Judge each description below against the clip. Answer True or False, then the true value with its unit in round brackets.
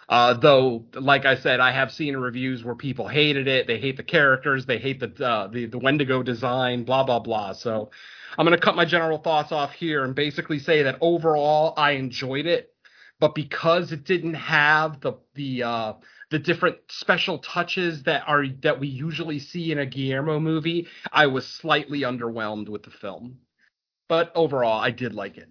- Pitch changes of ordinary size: True (3.9 semitones)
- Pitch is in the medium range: True (145 Hz)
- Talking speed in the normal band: True (190 wpm)